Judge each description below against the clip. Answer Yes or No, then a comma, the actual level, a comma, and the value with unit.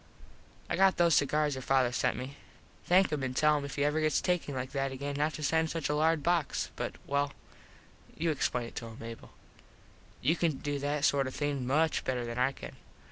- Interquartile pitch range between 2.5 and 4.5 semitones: Yes, average, 2.8 semitones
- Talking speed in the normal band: No, fast, 220 wpm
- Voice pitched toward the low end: No, medium, 145 Hz